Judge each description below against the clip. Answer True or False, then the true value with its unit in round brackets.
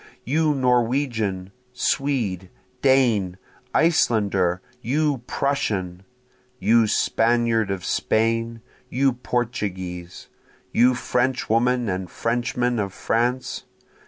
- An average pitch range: True (4.2 semitones)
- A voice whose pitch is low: True (115 Hz)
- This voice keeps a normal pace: False (80 wpm)